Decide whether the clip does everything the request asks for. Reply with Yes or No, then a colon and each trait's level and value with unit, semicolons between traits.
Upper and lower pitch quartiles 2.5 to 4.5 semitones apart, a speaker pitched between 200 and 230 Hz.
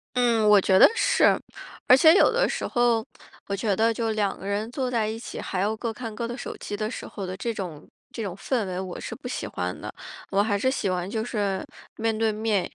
Yes: average, 2.8 semitones; high, 220 Hz